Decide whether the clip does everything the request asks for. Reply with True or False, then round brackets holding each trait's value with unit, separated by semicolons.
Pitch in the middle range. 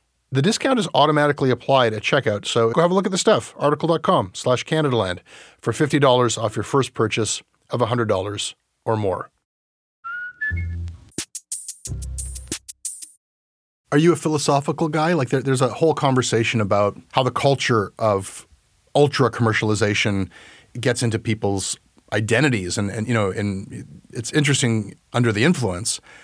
False (120 Hz)